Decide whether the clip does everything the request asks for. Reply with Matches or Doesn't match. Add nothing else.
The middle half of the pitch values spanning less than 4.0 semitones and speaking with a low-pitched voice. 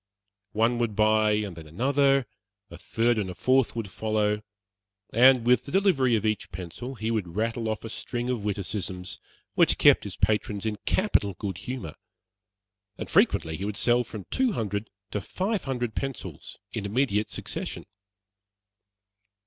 Matches